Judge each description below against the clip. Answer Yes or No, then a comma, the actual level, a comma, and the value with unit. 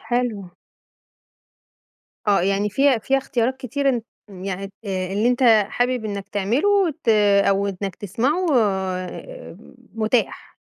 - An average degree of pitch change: Yes, average, 4.5 semitones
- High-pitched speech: Yes, high, 220 Hz